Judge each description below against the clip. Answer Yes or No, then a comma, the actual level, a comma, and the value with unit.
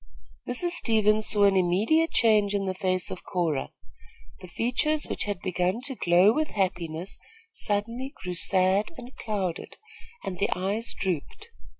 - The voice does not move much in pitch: No, average, 4.0 semitones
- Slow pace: No, average, 150 wpm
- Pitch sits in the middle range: No, high, 200 Hz